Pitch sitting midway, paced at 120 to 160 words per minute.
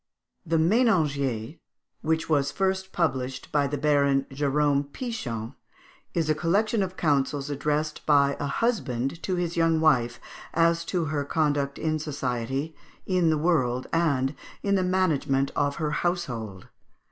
Yes: medium, 150 Hz; average, 140 wpm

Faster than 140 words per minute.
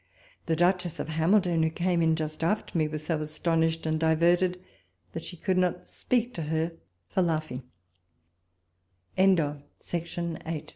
No: slow, 135 wpm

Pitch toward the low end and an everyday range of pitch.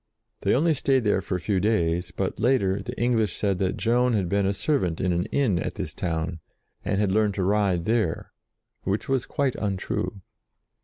Yes: low, 100 Hz; average, 4.3 semitones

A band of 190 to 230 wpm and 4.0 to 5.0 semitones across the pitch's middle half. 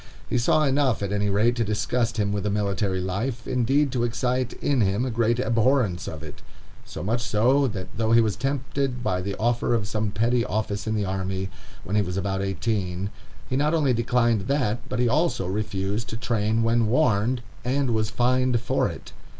No: average, 200 wpm; average, 3.5 semitones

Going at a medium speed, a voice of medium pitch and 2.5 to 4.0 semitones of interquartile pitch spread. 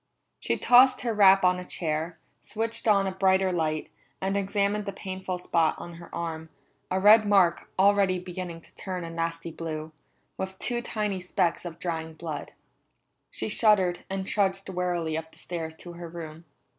Yes: average, 170 wpm; medium, 180 Hz; average, 2.8 semitones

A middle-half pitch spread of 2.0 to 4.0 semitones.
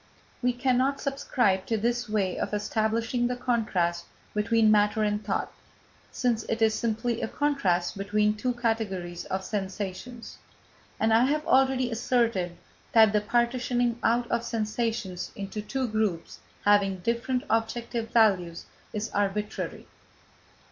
Yes: average, 2.8 semitones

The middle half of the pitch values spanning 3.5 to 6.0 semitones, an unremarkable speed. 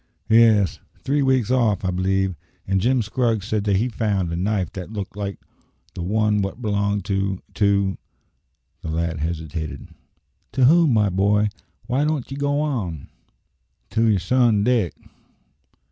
Yes: average, 3.8 semitones; average, 155 wpm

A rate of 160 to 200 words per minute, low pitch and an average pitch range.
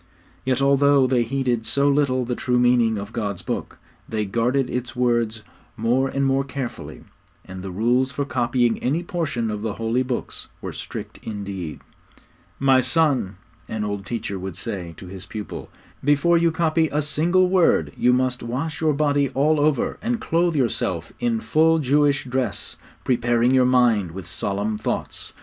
Yes: average, 165 wpm; low, 125 Hz; average, 4.4 semitones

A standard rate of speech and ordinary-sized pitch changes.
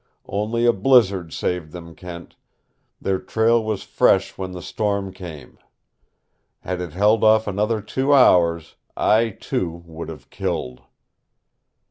No: slow, 130 wpm; average, 4.3 semitones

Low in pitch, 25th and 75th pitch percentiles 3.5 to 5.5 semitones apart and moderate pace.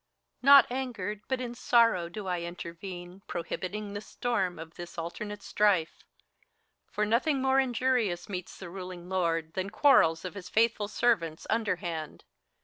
No: high, 195 Hz; average, 5.0 semitones; average, 145 wpm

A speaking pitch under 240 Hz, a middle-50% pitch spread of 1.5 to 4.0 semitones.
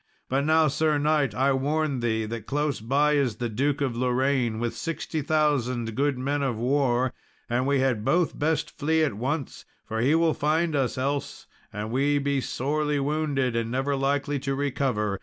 Yes: medium, 140 Hz; average, 3.0 semitones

